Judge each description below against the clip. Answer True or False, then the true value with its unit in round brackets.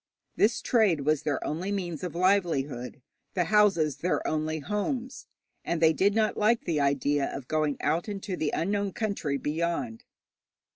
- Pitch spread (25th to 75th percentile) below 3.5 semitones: False (5.3 semitones)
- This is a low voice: False (170 Hz)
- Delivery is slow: False (155 wpm)